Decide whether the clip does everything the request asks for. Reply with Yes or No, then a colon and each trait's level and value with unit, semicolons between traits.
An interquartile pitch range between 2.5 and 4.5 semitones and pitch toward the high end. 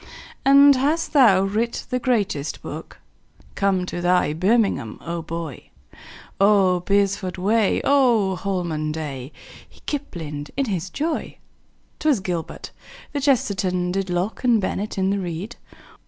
No: average, 5.0 semitones; high, 195 Hz